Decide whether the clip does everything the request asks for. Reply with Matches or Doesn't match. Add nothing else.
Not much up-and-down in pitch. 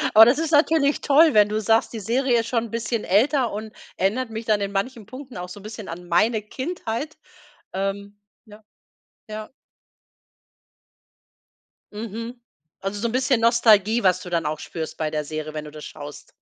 Doesn't match